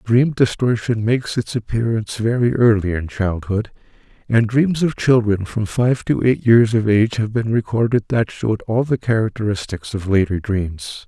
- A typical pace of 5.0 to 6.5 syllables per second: No, 4.8 syllables/s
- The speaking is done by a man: Yes, male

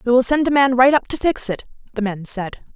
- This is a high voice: Yes, high, 245 Hz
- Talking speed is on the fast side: Yes, fast, 285 wpm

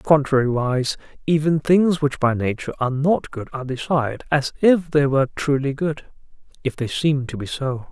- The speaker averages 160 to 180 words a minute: Yes, average, 175 wpm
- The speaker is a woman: No, male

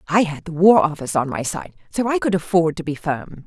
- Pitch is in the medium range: Yes, medium, 170 Hz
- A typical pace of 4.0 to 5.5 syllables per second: No, 5.7 syllables/s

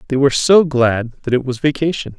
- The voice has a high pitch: No, low, 135 Hz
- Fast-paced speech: Yes, fast, 220 wpm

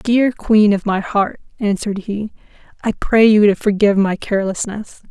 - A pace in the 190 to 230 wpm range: No, average, 165 wpm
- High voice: Yes, high, 205 Hz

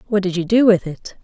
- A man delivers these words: No, female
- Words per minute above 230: Yes, fast, 290 wpm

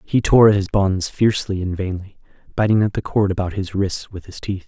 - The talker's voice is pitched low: Yes, very low, 95 Hz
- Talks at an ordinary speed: No, fast, 220 wpm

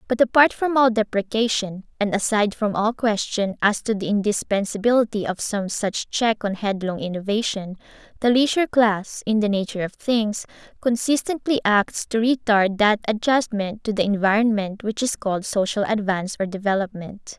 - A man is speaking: No, female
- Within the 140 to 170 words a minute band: Yes, average, 155 wpm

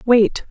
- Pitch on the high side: Yes, high, 230 Hz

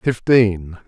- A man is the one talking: Yes, male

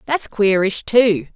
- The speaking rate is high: No, slow, 130 wpm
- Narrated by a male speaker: No, female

